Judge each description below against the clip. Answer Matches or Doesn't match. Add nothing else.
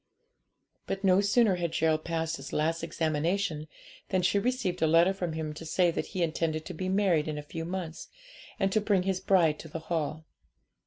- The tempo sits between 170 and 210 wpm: Matches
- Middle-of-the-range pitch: Matches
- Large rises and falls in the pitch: Doesn't match